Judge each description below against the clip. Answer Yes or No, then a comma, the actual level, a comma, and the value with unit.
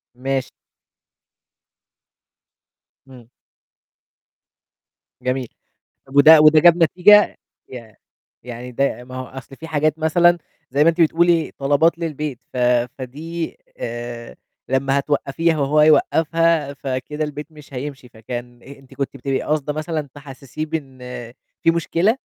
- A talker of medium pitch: Yes, medium, 145 Hz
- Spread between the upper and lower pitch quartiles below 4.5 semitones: Yes, average, 3.6 semitones